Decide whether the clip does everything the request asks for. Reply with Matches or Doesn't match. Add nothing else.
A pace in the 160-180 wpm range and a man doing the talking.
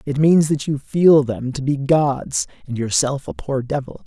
Doesn't match